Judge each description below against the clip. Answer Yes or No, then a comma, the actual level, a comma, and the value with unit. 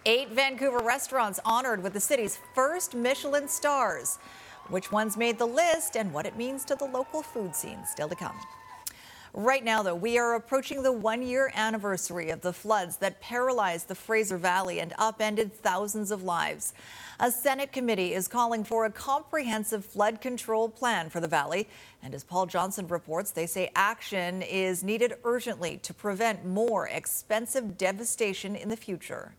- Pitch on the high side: Yes, high, 220 Hz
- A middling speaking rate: Yes, average, 170 wpm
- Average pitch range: Yes, average, 4.6 semitones